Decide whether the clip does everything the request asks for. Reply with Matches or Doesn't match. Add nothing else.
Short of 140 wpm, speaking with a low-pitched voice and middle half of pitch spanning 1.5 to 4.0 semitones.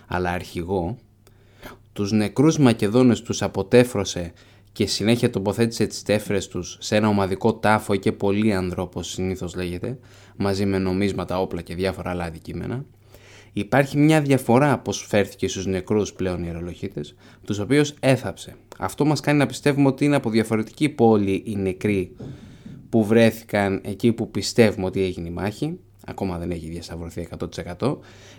Doesn't match